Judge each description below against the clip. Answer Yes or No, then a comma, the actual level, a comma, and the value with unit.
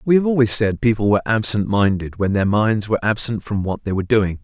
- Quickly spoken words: Yes, fast, 245 wpm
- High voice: No, low, 105 Hz